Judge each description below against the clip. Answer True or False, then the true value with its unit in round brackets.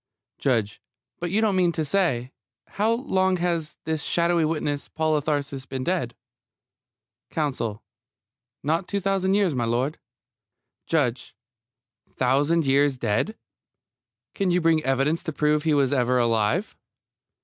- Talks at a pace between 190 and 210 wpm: False (135 wpm)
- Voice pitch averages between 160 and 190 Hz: False (150 Hz)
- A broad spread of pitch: False (4.8 semitones)